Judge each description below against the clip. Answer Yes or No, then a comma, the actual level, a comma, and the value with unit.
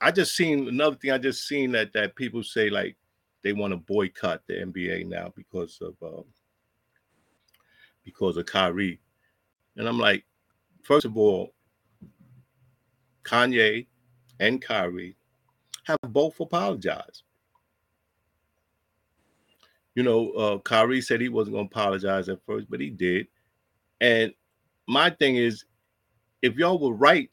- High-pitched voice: No, low, 110 Hz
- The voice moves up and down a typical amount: Yes, average, 4.5 semitones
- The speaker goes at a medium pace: No, slow, 130 wpm